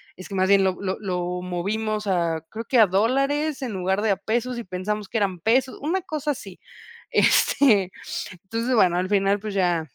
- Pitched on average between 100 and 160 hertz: No, high, 200 Hz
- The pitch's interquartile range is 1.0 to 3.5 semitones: No, average, 4.0 semitones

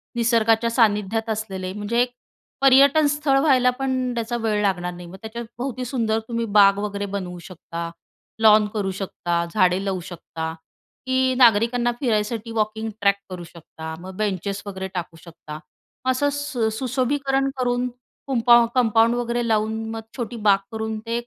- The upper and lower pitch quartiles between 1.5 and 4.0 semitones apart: Yes, average, 3.7 semitones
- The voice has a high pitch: Yes, high, 220 Hz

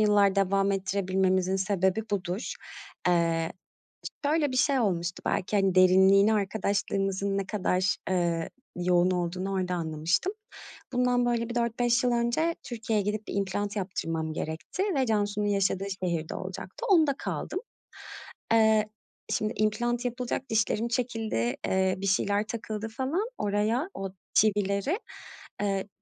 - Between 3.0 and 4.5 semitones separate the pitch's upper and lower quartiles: Yes, average, 3.7 semitones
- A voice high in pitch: Yes, high, 200 Hz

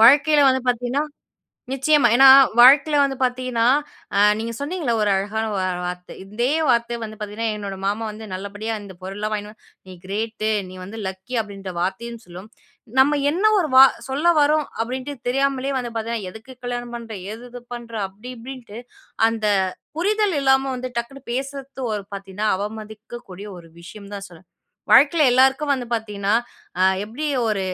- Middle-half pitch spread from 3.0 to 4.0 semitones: No, average, 4.5 semitones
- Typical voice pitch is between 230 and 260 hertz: Yes, high, 235 Hz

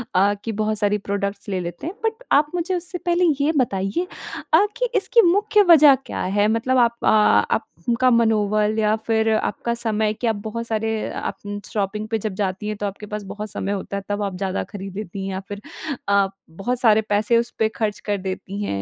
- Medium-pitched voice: No, high, 215 Hz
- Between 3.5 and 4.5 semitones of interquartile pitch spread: No, average, 2.9 semitones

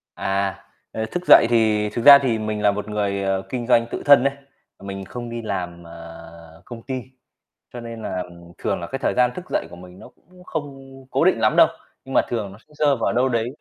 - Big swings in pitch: No, average, 4.9 semitones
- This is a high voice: No, low, 115 Hz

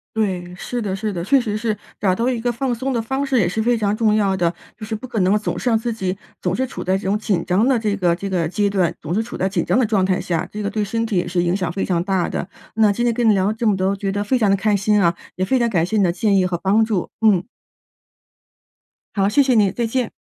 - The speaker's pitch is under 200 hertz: No, high, 205 Hz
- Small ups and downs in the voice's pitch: No, average, 3.3 semitones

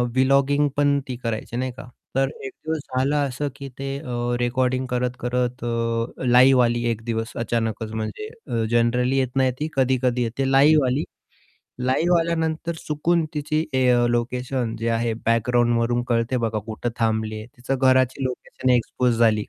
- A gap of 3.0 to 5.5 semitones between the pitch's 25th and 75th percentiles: No, narrow, 2.4 semitones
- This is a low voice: Yes, low, 125 Hz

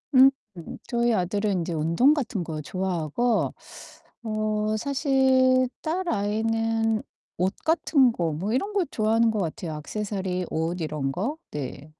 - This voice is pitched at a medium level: No, high, 215 Hz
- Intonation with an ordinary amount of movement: No, wide, 6.2 semitones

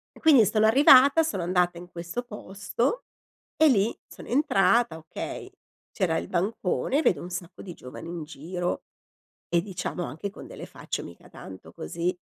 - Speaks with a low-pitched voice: No, medium, 185 Hz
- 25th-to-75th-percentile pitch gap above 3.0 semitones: Yes, wide, 5.6 semitones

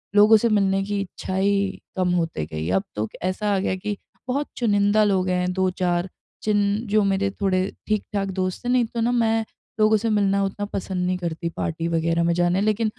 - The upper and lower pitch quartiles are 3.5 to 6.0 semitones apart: No, average, 2.7 semitones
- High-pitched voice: Yes, high, 195 Hz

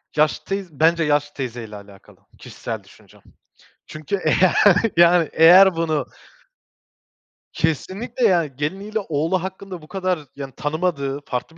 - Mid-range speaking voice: Yes, medium, 160 Hz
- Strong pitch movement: No, average, 4.2 semitones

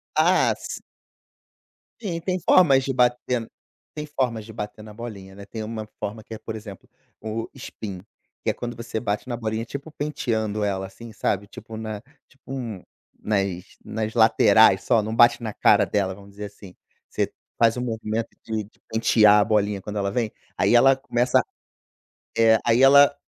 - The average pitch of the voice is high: No, low, 110 Hz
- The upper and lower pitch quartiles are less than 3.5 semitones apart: Yes, narrow, 2.5 semitones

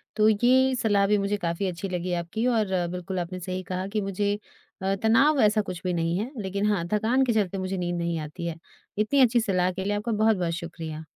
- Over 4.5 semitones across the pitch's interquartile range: No, average, 3.3 semitones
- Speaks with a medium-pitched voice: No, high, 195 Hz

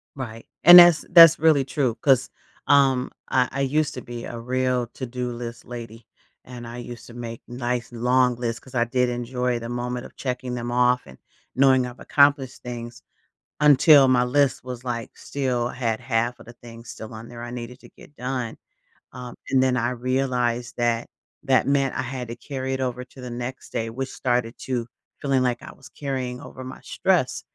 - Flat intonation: Yes, narrow, 1.7 semitones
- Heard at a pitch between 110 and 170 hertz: Yes, low, 125 Hz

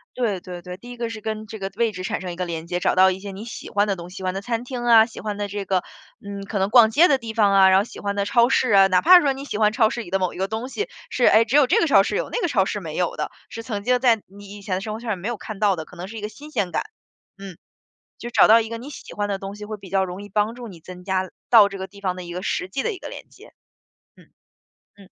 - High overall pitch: Yes, high, 205 Hz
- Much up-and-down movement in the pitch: No, average, 3.3 semitones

